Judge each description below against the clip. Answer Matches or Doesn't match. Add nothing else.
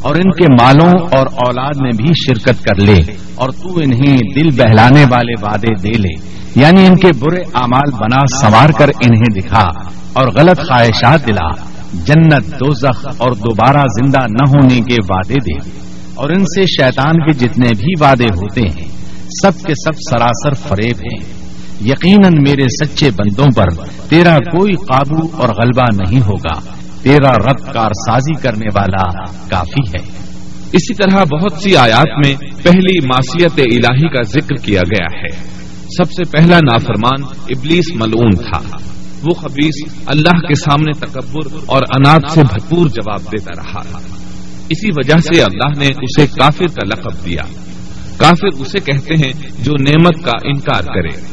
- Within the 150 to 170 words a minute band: Matches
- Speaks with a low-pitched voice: Matches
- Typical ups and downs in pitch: Doesn't match